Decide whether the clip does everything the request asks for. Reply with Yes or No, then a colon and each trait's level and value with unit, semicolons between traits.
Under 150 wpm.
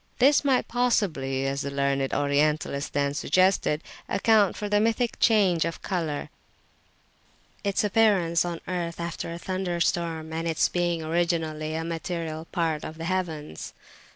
Yes: average, 140 wpm